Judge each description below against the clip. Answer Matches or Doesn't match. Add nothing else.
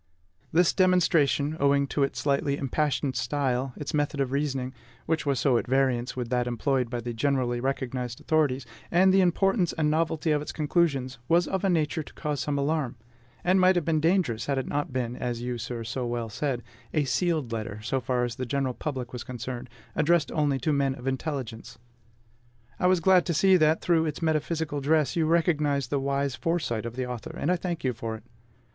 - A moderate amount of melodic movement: Matches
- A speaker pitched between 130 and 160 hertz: Matches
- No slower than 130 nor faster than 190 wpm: Doesn't match